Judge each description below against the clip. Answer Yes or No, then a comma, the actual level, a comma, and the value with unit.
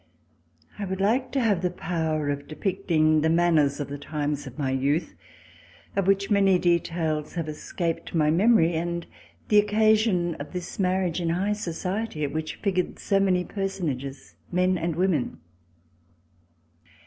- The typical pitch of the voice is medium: Yes, medium, 175 Hz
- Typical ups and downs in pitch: Yes, average, 3.9 semitones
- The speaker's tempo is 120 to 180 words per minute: Yes, average, 150 wpm